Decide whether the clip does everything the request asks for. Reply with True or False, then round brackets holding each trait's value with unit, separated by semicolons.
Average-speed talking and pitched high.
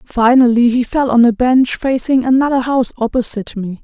True (170 wpm; 245 Hz)